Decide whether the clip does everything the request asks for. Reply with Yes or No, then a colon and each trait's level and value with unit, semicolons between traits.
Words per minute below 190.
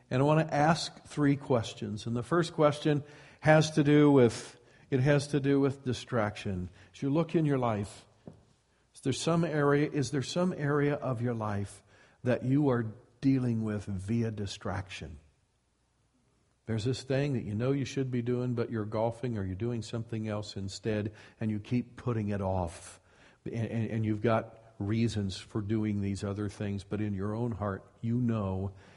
Yes: average, 180 wpm